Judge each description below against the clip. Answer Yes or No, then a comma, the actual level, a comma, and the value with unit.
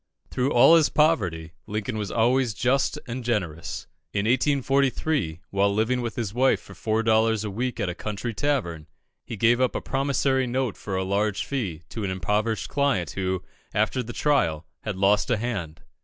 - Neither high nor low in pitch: No, low, 110 Hz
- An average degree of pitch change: Yes, average, 4.7 semitones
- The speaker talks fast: No, average, 180 wpm